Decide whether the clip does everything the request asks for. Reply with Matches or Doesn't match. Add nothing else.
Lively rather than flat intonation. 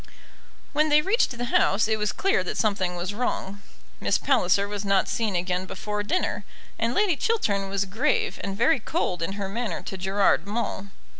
Doesn't match